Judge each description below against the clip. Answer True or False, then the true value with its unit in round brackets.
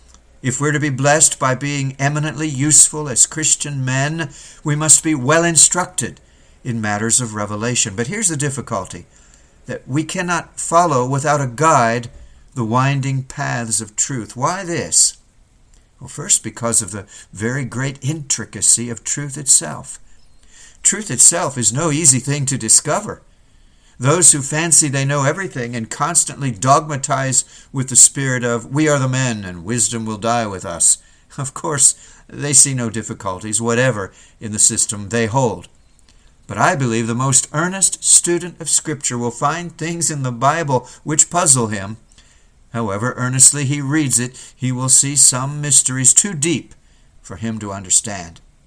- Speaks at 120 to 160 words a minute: True (155 wpm)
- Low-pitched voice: True (130 Hz)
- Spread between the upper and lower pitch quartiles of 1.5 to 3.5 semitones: False (4.5 semitones)